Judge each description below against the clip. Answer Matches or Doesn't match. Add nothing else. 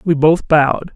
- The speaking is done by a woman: Doesn't match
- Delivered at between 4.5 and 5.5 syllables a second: Matches